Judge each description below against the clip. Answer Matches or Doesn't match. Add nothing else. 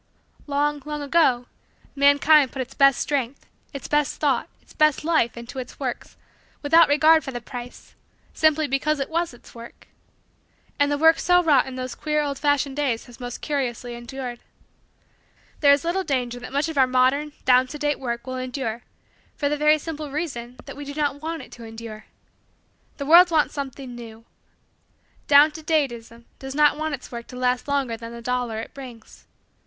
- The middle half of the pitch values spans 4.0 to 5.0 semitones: Doesn't match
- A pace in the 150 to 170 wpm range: Doesn't match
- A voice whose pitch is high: Matches